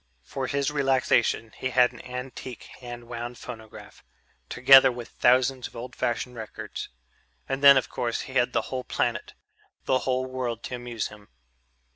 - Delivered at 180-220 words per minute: No, average, 160 wpm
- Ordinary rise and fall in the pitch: No, narrow, 1.5 semitones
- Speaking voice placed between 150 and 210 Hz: No, low, 125 Hz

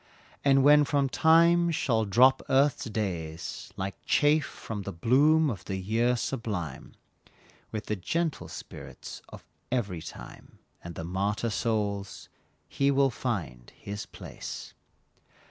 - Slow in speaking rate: Yes, slow, 130 wpm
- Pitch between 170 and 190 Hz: No, low, 115 Hz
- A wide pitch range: Yes, wide, 6.1 semitones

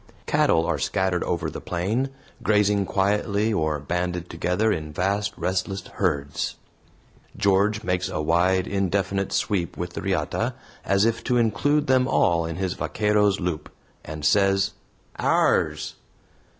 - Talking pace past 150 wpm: No, slow, 135 wpm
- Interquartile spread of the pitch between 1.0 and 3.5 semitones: Yes, average, 3.1 semitones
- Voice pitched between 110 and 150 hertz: No, very low, 95 Hz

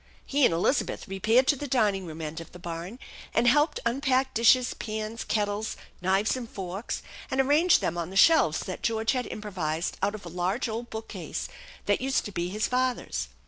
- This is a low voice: No, high, 220 Hz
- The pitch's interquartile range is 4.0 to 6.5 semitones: Yes, wide, 5.6 semitones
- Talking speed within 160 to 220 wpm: Yes, average, 190 wpm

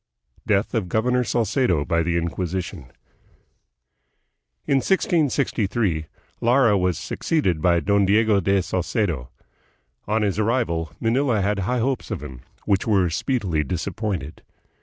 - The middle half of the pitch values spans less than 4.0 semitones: No, average, 5.3 semitones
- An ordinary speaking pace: No, slow, 120 wpm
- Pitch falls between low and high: No, low, 100 Hz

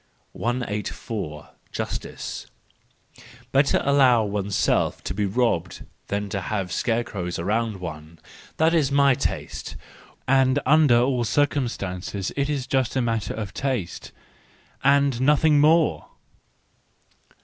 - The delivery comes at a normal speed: No, slow, 100 wpm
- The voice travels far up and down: Yes, wide, 5.7 semitones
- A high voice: No, low, 120 Hz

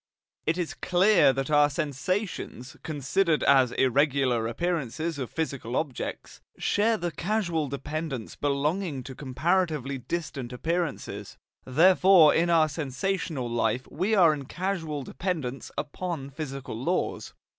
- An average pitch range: Yes, average, 4.6 semitones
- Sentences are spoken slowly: Yes, slow, 120 wpm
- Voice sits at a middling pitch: Yes, medium, 150 Hz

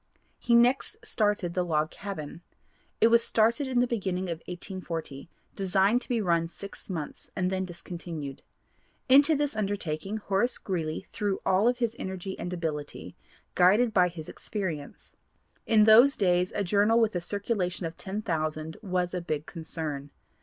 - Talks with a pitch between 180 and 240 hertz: Yes, high, 190 Hz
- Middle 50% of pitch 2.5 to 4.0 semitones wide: No, average, 4.5 semitones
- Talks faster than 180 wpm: No, average, 155 wpm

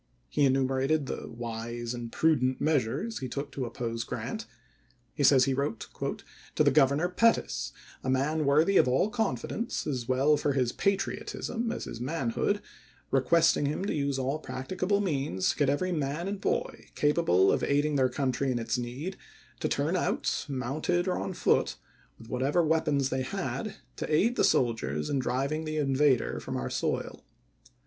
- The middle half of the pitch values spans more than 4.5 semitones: No, average, 3.8 semitones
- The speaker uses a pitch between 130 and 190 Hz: Yes, medium, 140 Hz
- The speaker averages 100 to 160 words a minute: No, average, 175 wpm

